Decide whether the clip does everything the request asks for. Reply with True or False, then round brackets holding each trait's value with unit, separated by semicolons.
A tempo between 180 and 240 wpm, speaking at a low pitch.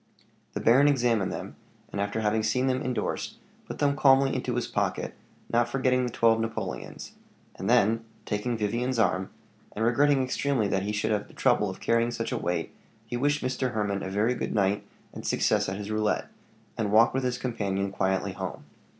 True (190 wpm; 115 Hz)